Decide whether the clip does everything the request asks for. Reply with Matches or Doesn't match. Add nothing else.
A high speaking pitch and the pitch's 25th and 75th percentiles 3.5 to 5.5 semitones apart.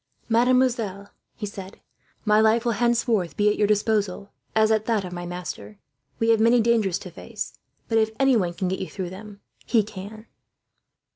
Doesn't match